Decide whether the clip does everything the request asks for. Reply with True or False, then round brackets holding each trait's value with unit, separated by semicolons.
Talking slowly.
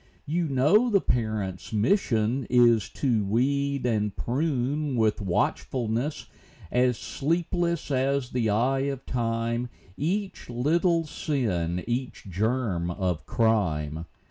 True (110 wpm)